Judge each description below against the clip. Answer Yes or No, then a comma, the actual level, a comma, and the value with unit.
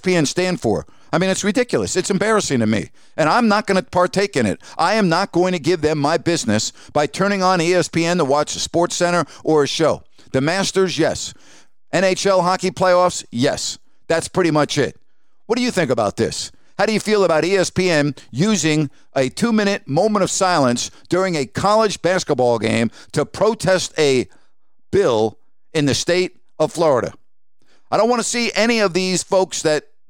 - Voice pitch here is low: No, medium, 175 Hz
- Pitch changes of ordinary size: Yes, average, 4.4 semitones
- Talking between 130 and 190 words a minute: Yes, average, 185 wpm